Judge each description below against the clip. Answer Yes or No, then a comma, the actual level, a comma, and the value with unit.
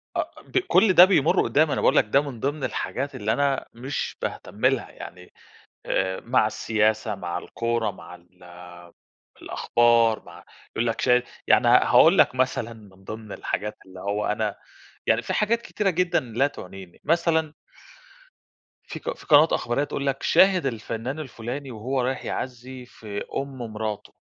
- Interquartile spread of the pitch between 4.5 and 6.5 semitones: Yes, average, 4.8 semitones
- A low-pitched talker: Yes, low, 120 Hz